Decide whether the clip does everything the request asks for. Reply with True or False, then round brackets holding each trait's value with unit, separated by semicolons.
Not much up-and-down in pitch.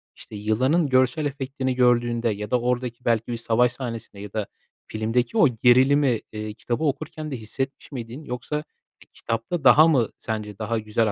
False (3.2 semitones)